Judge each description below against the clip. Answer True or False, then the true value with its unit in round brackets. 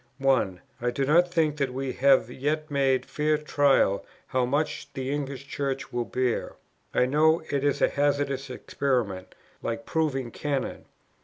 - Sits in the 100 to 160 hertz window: True (140 Hz)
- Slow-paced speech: False (155 wpm)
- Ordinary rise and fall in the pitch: False (2.2 semitones)